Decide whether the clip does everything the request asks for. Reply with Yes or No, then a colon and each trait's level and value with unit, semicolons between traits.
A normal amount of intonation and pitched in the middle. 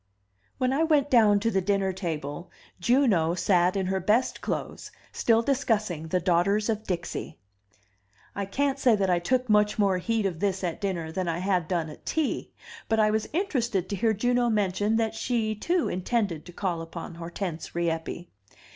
No: average, 4.6 semitones; high, 200 Hz